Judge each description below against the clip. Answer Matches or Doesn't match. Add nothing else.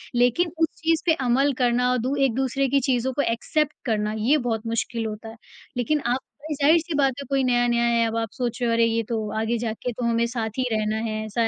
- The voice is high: Matches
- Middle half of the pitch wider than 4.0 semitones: Doesn't match